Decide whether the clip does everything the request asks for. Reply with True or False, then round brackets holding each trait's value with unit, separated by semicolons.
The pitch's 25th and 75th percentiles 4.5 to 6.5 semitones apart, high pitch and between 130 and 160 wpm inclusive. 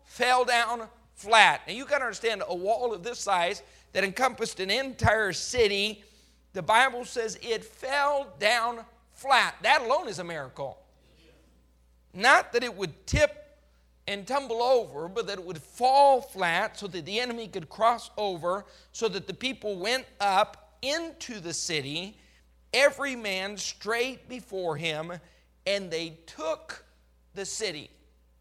True (5.3 semitones; 220 Hz; 150 wpm)